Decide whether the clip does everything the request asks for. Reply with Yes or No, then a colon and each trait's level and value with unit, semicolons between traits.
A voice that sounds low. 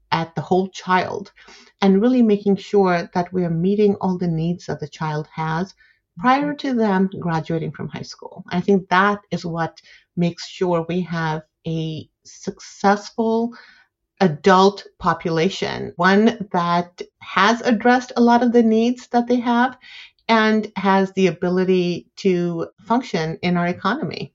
No: high, 190 Hz